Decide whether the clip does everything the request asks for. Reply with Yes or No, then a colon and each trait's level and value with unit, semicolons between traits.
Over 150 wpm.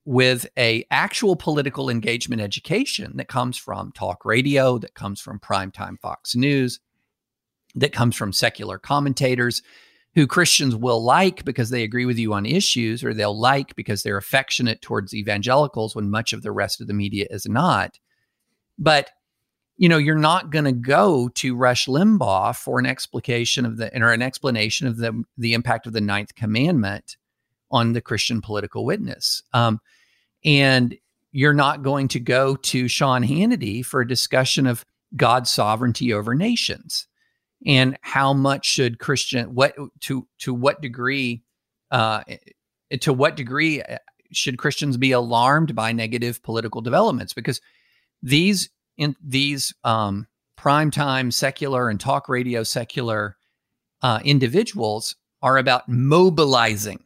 No: average, 145 wpm